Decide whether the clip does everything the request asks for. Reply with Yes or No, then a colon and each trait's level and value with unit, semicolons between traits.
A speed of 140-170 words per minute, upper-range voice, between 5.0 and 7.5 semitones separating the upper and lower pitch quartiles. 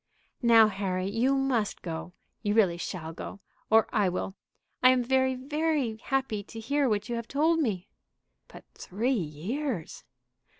Yes: average, 155 wpm; high, 225 Hz; average, 5.3 semitones